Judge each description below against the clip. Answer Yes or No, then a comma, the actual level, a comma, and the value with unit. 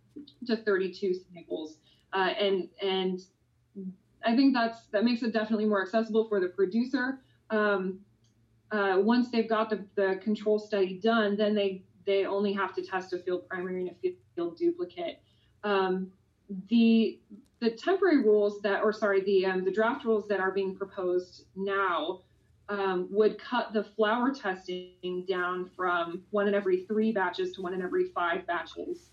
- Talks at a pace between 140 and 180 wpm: Yes, average, 165 wpm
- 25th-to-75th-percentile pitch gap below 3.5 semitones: Yes, average, 3.0 semitones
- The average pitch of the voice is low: No, high, 200 Hz